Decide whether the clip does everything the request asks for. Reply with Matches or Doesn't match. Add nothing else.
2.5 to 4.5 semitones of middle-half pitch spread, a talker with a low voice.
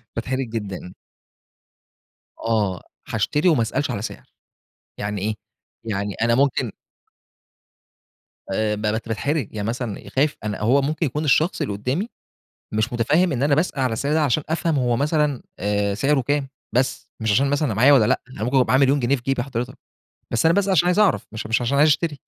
Doesn't match